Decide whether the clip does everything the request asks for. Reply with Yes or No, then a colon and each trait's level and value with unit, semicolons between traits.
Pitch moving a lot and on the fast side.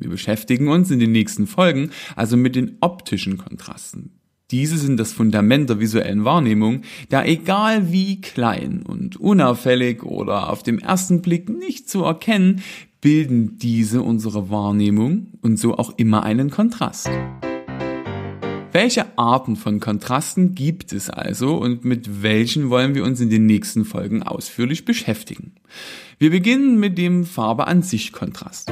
No: wide, 8.1 semitones; average, 145 wpm